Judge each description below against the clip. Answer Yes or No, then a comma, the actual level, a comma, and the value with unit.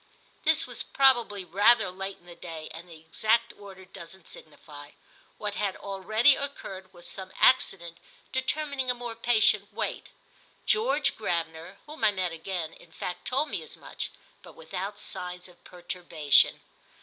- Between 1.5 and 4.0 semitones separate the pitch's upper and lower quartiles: No, wide, 5.4 semitones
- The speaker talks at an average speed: Yes, average, 150 wpm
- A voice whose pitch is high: Yes, high, 195 Hz